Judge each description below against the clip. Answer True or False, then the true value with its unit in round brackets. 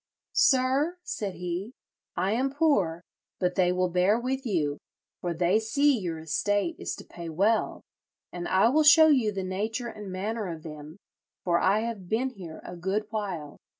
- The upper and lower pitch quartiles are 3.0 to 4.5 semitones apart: False (4.9 semitones)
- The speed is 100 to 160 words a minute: False (175 wpm)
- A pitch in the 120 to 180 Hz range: False (195 Hz)